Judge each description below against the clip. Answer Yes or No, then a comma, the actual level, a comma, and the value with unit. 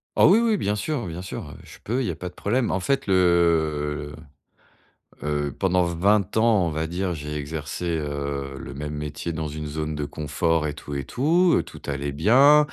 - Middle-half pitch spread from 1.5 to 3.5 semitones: No, average, 5.2 semitones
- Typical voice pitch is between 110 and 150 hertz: No, very low, 80 Hz